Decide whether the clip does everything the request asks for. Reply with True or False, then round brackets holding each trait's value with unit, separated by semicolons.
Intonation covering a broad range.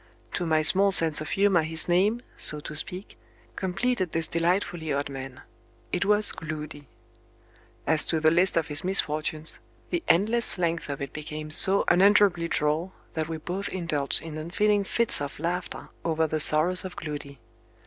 False (3.6 semitones)